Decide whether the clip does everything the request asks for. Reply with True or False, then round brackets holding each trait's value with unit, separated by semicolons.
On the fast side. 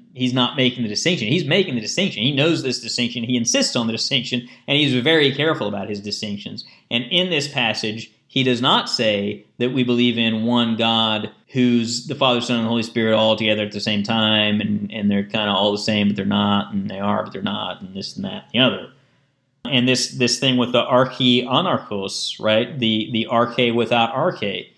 True (220 wpm)